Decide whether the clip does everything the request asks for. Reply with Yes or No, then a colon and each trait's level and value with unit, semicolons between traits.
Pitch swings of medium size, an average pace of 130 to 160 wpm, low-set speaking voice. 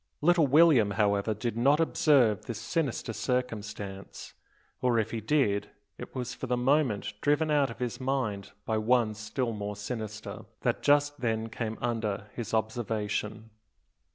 Yes: average, 3.6 semitones; average, 150 wpm; low, 115 Hz